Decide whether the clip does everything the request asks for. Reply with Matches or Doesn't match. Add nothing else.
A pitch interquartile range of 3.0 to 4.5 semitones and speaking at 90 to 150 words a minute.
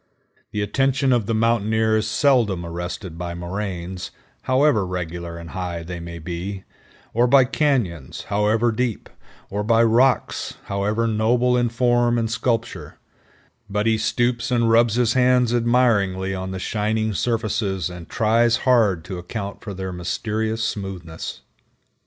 Matches